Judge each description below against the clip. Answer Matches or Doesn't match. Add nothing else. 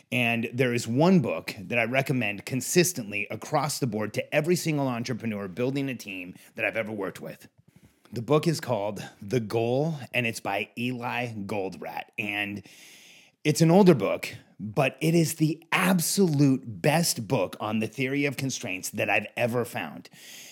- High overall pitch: Doesn't match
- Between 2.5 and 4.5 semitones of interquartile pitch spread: Doesn't match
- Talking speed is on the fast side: Doesn't match